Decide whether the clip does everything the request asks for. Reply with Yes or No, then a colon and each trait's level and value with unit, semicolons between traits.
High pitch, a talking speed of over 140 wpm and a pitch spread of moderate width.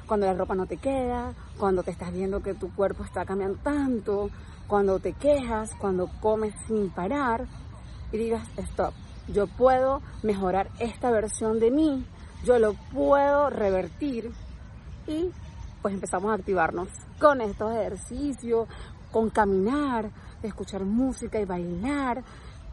No: high, 220 Hz; average, 135 wpm; average, 4.5 semitones